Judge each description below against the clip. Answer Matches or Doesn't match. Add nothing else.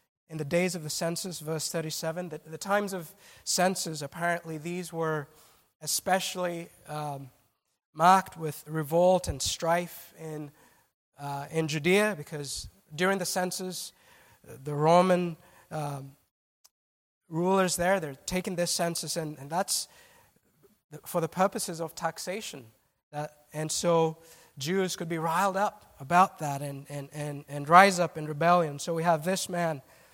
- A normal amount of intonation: Matches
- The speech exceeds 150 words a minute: Doesn't match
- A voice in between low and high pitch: Matches